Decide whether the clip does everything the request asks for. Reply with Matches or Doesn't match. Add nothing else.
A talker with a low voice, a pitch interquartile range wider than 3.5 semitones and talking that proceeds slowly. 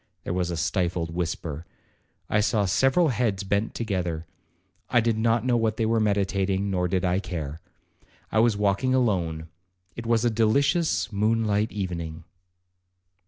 Doesn't match